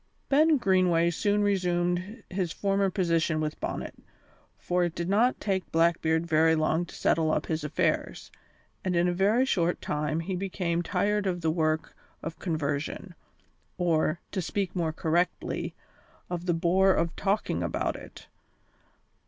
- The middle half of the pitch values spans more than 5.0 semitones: No, average, 2.8 semitones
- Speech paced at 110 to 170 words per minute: Yes, average, 150 wpm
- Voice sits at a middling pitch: Yes, medium, 175 Hz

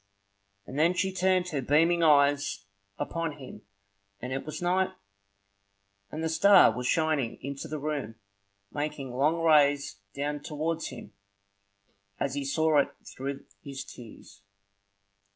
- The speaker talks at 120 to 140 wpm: Yes, slow, 135 wpm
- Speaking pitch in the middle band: Yes, medium, 145 Hz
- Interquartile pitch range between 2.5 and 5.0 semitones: Yes, average, 2.9 semitones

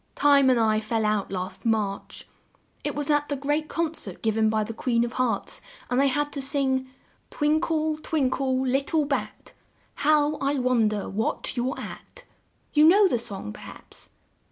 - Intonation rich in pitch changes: No, average, 4.8 semitones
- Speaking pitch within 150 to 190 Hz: No, very high, 260 Hz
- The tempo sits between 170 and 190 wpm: Yes, average, 185 wpm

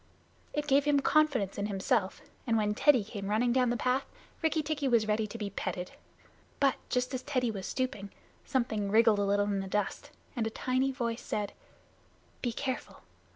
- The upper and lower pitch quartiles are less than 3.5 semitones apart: No, average, 4.1 semitones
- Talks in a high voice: Yes, high, 235 Hz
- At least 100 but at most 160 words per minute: No, average, 185 wpm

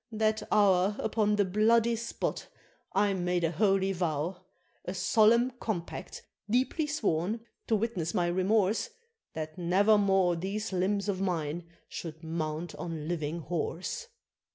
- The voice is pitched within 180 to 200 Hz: Yes, high, 190 Hz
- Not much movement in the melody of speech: No, average, 3.9 semitones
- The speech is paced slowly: Yes, slow, 130 wpm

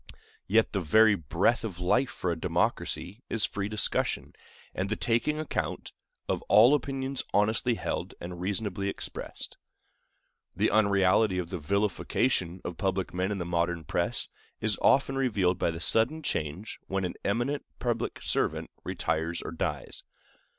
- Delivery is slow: No, average, 150 wpm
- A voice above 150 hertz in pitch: No, low, 100 Hz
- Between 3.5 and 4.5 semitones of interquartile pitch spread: Yes, average, 4.2 semitones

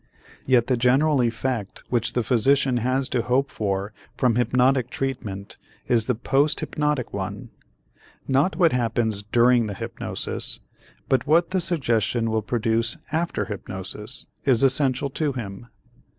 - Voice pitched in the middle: No, low, 125 Hz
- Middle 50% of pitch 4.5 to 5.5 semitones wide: No, average, 3.2 semitones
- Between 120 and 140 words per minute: Yes, slow, 135 wpm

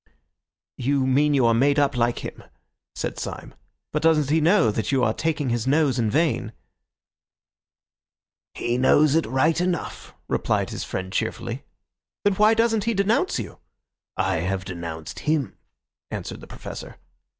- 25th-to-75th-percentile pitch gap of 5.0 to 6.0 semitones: Yes, wide, 5.5 semitones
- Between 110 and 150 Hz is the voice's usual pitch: Yes, medium, 140 Hz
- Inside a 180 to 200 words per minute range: No, average, 150 wpm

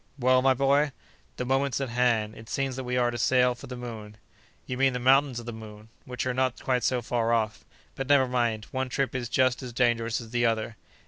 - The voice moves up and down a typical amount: No, narrow, 2.0 semitones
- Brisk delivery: Yes, fast, 235 wpm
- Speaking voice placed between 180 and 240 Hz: No, low, 125 Hz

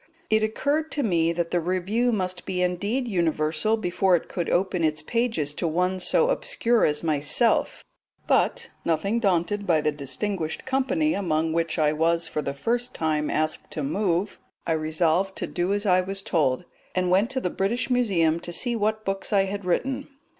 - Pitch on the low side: No, medium, 185 Hz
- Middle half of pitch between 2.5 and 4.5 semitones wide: No, average, 5.0 semitones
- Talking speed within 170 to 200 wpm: Yes, average, 180 wpm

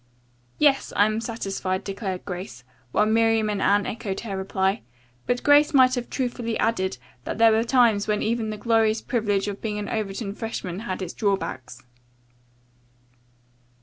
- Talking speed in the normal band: Yes, average, 155 wpm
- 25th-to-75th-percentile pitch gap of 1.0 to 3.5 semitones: Yes, average, 2.8 semitones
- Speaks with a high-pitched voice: Yes, high, 215 Hz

